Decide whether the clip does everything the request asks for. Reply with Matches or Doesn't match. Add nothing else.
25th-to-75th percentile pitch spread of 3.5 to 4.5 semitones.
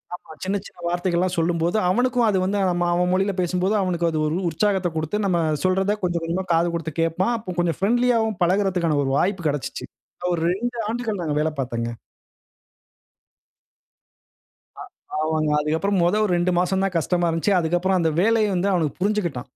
Doesn't match